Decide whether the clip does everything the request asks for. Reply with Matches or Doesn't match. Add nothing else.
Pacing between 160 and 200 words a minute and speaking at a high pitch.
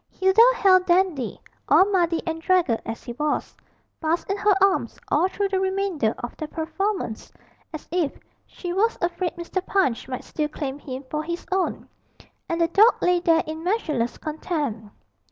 Matches